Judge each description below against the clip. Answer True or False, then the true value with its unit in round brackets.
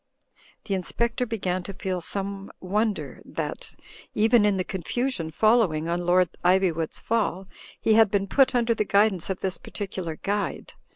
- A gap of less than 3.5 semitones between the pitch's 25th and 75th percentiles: True (3.1 semitones)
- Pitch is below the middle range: False (195 Hz)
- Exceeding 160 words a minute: False (155 wpm)